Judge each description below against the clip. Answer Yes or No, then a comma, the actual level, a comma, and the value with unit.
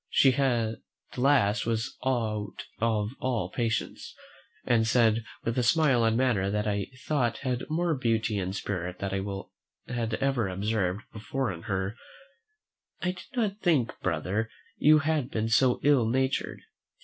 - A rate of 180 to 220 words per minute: No, average, 150 wpm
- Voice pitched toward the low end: Yes, low, 115 Hz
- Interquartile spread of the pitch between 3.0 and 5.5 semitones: Yes, average, 4.2 semitones